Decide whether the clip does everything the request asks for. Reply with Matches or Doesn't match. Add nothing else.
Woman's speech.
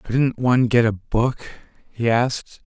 Doesn't match